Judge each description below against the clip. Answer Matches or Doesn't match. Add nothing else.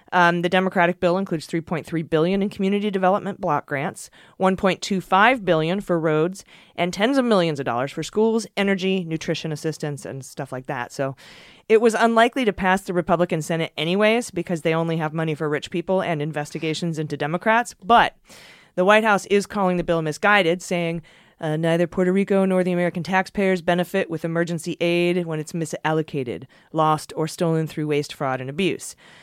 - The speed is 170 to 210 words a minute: Matches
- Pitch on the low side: Doesn't match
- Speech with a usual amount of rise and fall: Matches